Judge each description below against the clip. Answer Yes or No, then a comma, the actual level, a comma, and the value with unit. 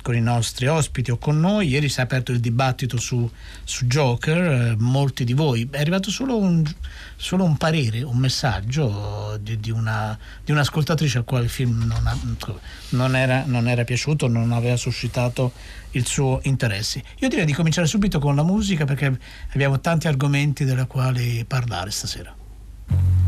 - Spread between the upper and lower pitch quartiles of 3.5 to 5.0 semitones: Yes, average, 4.0 semitones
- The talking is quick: Yes, fast, 175 wpm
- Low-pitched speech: Yes, low, 130 Hz